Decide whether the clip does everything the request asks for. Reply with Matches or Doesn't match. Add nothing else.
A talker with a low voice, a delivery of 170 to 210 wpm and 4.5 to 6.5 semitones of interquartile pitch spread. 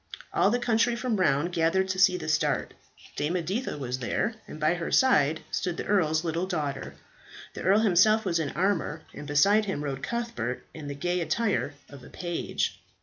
Doesn't match